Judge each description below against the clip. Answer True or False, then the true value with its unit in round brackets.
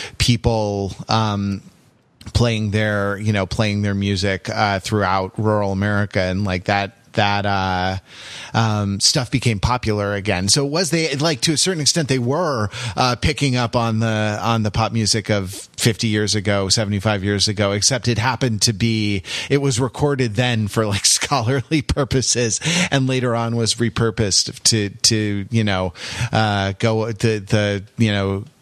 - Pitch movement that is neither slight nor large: True (3.4 semitones)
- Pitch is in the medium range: False (110 Hz)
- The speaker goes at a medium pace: True (165 wpm)